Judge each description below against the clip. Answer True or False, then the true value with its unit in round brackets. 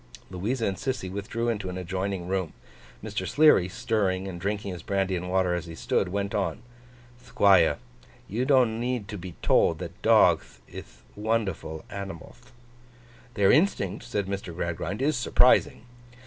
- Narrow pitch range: False (3.7 semitones)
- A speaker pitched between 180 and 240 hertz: False (100 Hz)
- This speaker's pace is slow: False (150 wpm)